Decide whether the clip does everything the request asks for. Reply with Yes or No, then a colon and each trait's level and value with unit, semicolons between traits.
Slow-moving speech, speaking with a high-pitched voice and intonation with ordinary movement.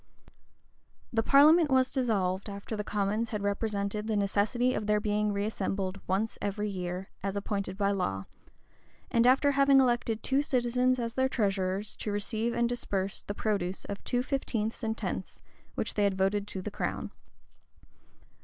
No: average, 160 wpm; high, 210 Hz; average, 3.3 semitones